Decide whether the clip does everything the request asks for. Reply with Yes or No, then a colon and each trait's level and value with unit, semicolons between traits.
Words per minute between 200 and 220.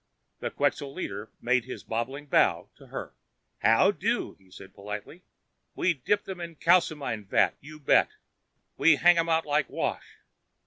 No: average, 160 wpm